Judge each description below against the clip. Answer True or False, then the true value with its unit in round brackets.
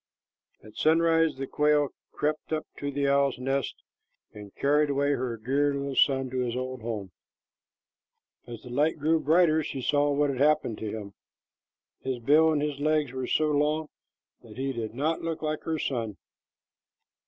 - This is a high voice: False (140 Hz)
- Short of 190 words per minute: True (170 wpm)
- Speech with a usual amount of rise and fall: True (3.2 semitones)